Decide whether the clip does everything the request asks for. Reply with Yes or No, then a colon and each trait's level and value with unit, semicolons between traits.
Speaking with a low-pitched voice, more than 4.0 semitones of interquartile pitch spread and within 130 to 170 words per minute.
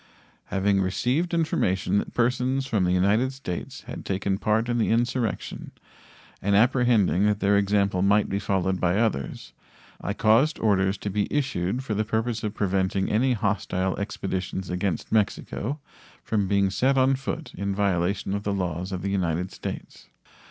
No: low, 100 Hz; average, 3.5 semitones; average, 160 wpm